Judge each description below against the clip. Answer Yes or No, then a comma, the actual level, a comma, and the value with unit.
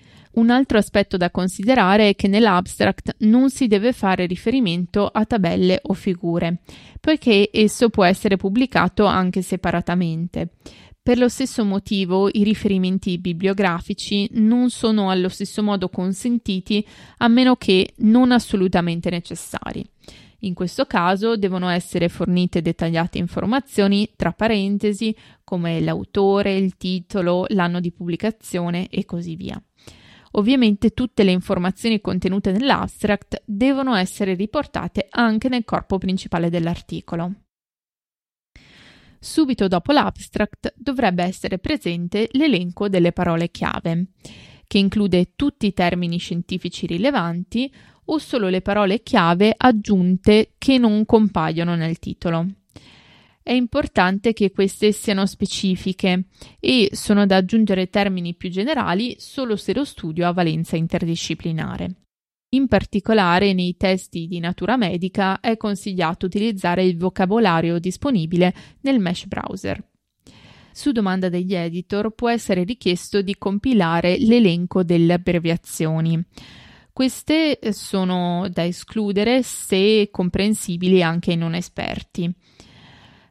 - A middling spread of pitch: Yes, average, 3.5 semitones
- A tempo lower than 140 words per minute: Yes, slow, 115 wpm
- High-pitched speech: Yes, high, 195 Hz